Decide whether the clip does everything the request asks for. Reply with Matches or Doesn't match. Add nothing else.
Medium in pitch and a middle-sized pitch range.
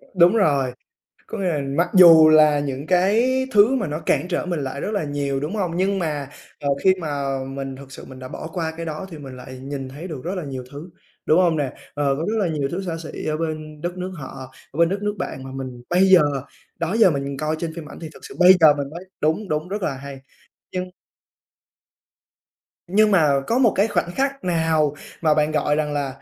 Matches